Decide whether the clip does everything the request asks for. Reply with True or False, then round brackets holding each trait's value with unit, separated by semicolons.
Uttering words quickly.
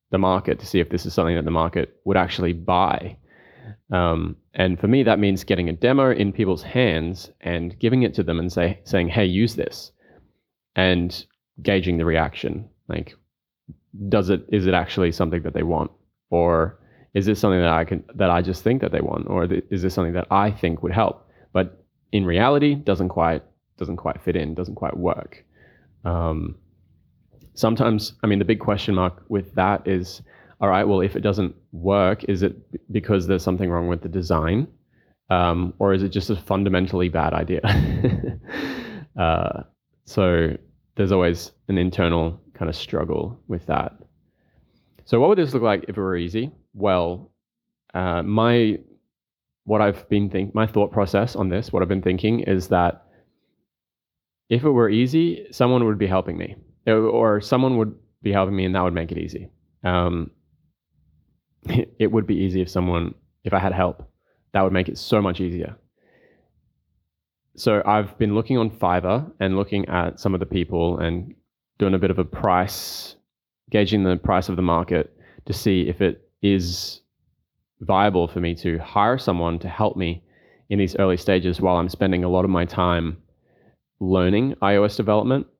False (180 wpm)